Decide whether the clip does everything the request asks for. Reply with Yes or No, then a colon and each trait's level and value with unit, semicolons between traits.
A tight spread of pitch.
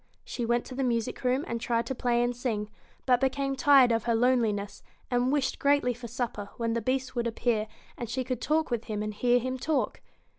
Yes: narrow, 2.1 semitones